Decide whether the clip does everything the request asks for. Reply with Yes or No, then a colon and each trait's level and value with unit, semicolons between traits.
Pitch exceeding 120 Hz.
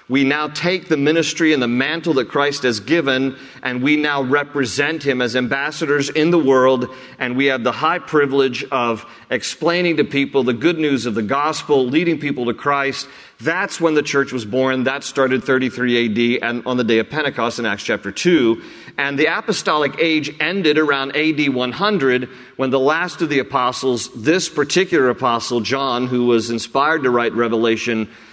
Yes: low, 135 Hz